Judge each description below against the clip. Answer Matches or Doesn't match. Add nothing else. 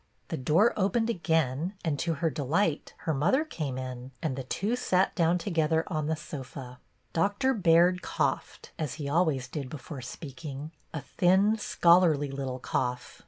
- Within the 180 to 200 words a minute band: Doesn't match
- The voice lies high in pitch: Doesn't match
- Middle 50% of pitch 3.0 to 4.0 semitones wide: Doesn't match